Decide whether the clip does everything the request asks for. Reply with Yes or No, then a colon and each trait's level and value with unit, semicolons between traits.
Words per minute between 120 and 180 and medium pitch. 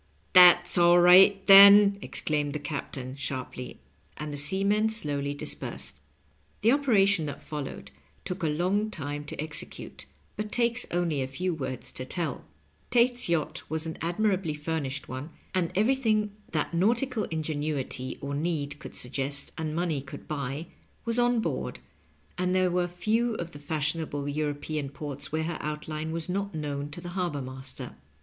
Yes: average, 160 wpm; medium, 160 Hz